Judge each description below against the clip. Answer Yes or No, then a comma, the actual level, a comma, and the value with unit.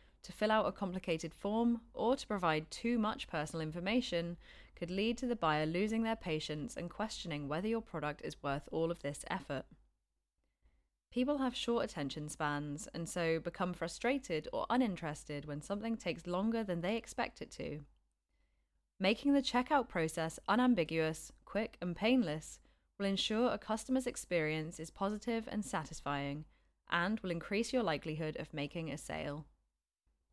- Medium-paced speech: Yes, average, 155 wpm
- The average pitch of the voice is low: No, medium, 175 Hz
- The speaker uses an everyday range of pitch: No, wide, 6.3 semitones